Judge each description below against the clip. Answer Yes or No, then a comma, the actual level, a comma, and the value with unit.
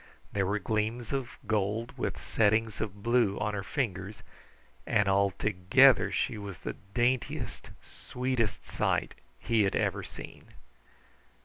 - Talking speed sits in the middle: No, slow, 125 wpm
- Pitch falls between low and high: No, low, 105 Hz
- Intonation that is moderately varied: Yes, average, 3.0 semitones